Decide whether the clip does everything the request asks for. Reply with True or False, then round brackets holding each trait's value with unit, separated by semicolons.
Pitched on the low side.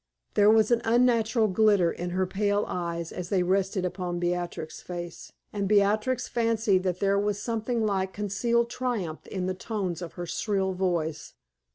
False (195 Hz)